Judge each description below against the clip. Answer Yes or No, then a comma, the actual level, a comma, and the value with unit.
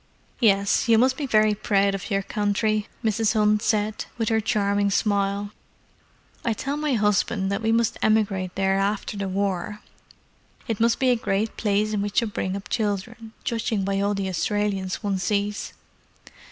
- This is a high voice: Yes, high, 205 Hz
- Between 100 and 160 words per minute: No, average, 170 wpm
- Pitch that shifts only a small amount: Yes, narrow, 1.9 semitones